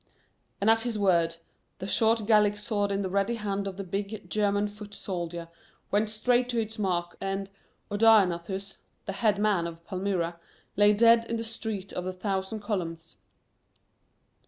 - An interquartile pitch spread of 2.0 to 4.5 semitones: Yes, narrow, 2.5 semitones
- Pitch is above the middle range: Yes, high, 200 Hz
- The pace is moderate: Yes, average, 160 wpm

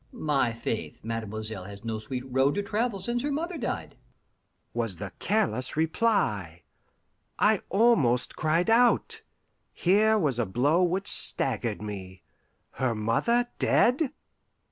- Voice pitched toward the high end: No, medium, 140 Hz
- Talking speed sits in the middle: No, slow, 125 wpm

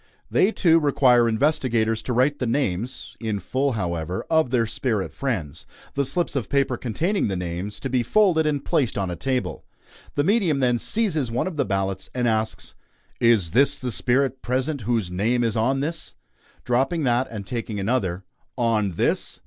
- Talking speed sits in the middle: Yes, average, 175 wpm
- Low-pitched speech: Yes, low, 125 Hz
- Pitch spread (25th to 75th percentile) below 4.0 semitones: No, average, 4.4 semitones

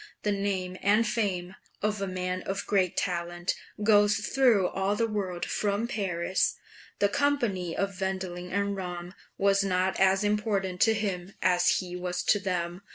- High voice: Yes, high, 195 Hz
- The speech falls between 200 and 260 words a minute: No, average, 160 wpm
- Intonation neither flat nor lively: No, narrow, 2.2 semitones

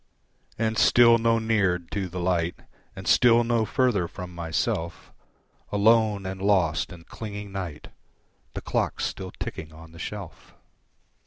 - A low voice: Yes, very low, 95 Hz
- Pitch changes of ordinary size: Yes, average, 4.5 semitones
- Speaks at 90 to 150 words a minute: Yes, average, 140 wpm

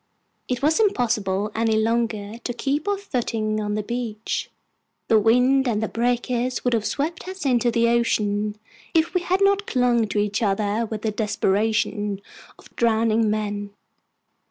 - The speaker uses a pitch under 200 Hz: No, high, 230 Hz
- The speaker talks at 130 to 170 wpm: Yes, average, 155 wpm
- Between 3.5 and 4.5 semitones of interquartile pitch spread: No, average, 2.8 semitones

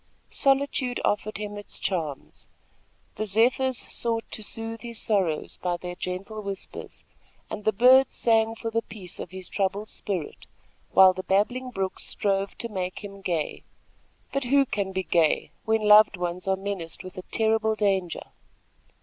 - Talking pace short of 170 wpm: Yes, average, 160 wpm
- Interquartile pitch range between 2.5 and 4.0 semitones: Yes, average, 3.2 semitones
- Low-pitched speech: No, high, 205 Hz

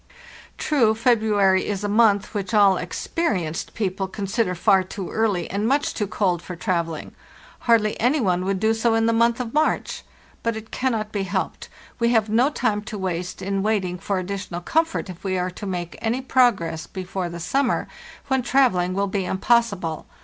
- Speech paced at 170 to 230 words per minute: Yes, average, 185 wpm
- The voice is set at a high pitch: Yes, high, 205 Hz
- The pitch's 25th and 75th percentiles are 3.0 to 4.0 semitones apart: Yes, average, 3.7 semitones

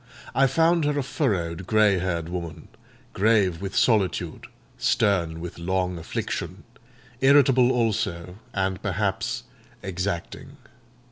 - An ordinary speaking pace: No, slow, 110 wpm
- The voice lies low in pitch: Yes, very low, 95 Hz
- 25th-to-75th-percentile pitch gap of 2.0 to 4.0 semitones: No, average, 4.6 semitones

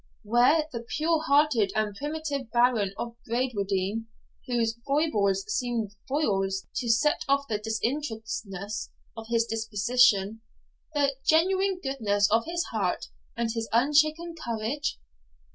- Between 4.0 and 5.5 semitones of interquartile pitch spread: Yes, average, 4.9 semitones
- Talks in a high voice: Yes, high, 235 Hz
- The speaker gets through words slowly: Yes, slow, 120 wpm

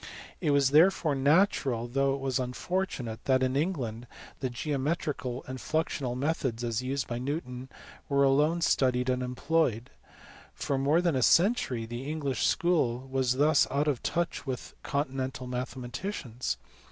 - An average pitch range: Yes, average, 3.1 semitones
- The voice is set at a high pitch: No, low, 135 Hz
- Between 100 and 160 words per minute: Yes, average, 145 wpm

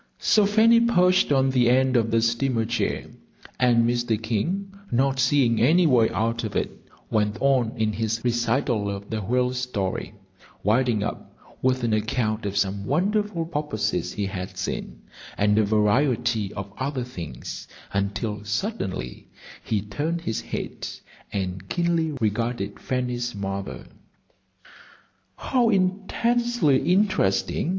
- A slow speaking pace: Yes, slow, 130 wpm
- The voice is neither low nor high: No, low, 120 Hz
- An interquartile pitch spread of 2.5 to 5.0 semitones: No, wide, 5.4 semitones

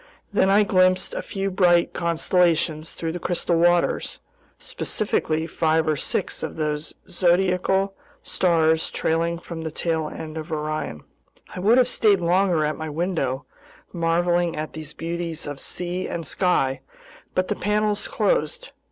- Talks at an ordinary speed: Yes, average, 145 wpm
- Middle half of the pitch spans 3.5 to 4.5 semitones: No, narrow, 2.6 semitones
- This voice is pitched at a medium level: Yes, medium, 170 Hz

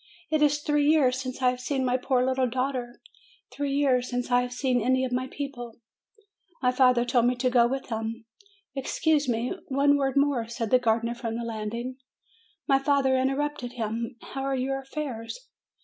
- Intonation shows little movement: Yes, narrow, 2.2 semitones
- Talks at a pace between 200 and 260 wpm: No, average, 190 wpm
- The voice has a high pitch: Yes, very high, 255 Hz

